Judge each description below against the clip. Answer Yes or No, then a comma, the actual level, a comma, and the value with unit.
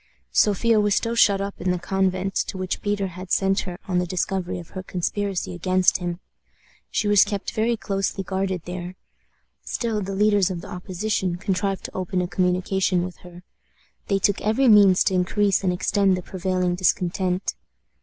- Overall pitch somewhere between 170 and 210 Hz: Yes, high, 190 Hz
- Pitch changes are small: Yes, narrow, 1.9 semitones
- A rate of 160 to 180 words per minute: Yes, average, 175 wpm